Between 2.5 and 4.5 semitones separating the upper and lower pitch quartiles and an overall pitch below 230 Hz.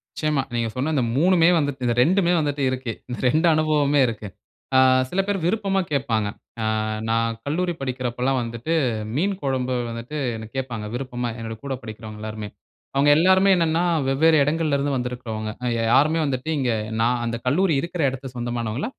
No: average, 4.9 semitones; low, 135 Hz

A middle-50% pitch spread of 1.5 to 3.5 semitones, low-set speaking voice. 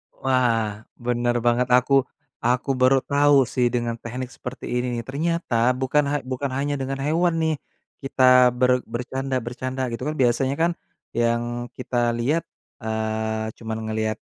Yes: narrow, 2.6 semitones; low, 125 Hz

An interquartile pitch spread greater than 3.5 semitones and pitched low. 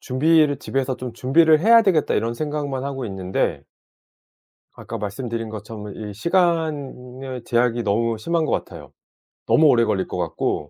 Yes: wide, 5.4 semitones; low, 125 Hz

